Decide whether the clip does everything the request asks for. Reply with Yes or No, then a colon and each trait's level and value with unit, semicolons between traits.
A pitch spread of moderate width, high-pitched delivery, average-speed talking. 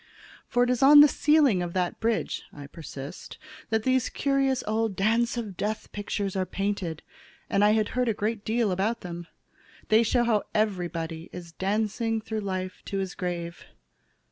Yes: average, 4.1 semitones; high, 210 Hz; average, 170 wpm